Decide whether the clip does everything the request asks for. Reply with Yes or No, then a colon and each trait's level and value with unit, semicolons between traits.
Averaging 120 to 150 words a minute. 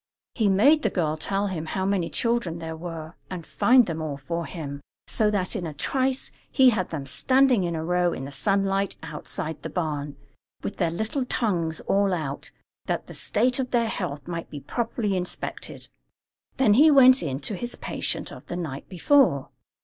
No: average, 190 wpm